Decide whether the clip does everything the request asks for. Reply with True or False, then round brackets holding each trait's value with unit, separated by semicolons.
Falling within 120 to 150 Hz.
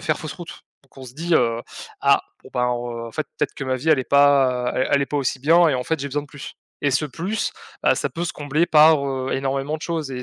True (140 Hz)